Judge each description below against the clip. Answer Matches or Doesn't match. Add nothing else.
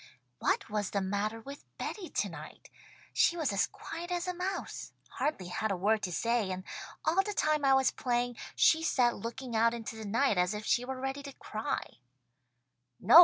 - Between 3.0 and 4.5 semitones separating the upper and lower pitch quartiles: Doesn't match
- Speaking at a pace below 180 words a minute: Doesn't match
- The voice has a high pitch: Matches